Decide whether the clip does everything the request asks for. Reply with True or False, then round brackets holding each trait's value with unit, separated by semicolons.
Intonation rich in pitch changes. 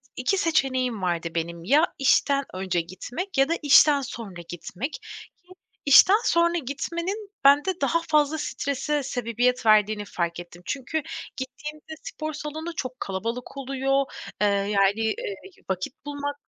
True (6.6 semitones)